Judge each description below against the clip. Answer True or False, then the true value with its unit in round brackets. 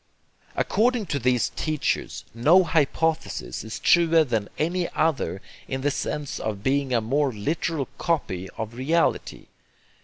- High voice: False (140 Hz)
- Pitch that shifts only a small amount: False (5.6 semitones)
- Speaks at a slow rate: True (130 wpm)